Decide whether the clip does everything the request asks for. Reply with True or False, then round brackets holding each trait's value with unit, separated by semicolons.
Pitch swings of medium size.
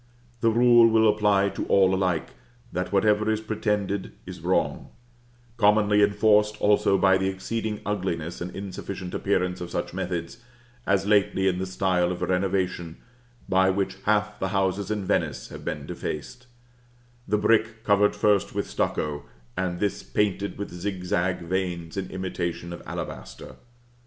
False (2.3 semitones)